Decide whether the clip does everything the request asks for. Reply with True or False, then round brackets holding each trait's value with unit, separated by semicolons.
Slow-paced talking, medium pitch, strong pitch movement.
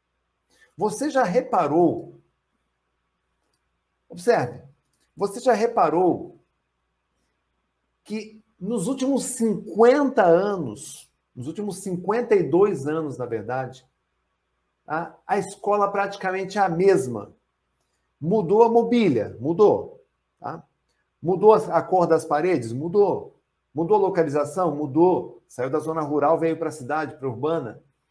True (105 wpm; 180 Hz; 6.7 semitones)